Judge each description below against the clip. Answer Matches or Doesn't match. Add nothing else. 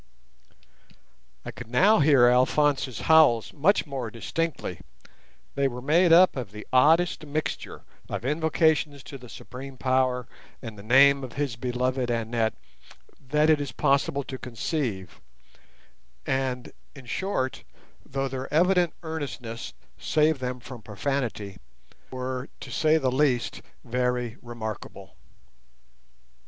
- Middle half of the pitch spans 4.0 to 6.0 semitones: Doesn't match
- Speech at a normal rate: Doesn't match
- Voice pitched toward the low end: Matches